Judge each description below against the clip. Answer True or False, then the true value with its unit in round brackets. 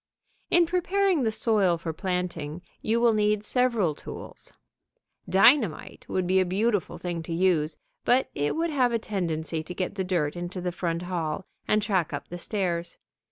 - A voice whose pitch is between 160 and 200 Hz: True (185 Hz)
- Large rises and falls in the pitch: False (4.6 semitones)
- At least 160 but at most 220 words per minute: True (170 wpm)